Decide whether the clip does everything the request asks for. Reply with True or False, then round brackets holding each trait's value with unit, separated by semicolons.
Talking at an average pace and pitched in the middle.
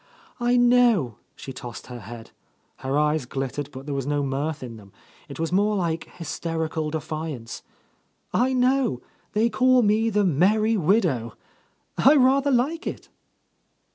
True (155 wpm; 165 Hz)